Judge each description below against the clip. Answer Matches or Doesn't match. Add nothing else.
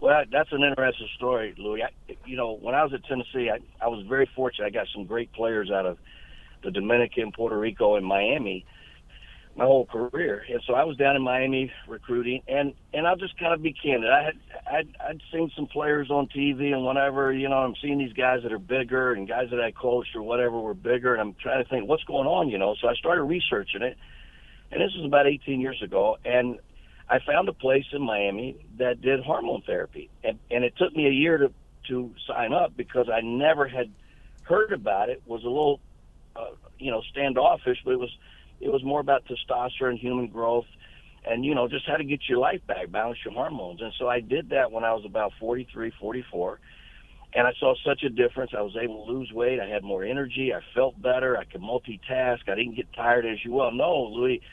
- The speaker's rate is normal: Doesn't match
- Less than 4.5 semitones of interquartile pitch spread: Matches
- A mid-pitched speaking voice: Doesn't match